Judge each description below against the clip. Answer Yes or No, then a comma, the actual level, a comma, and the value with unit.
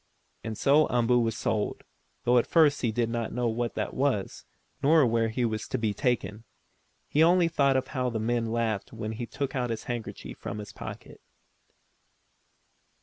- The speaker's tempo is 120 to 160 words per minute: No, average, 180 wpm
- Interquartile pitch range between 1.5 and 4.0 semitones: Yes, average, 2.8 semitones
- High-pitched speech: No, low, 120 Hz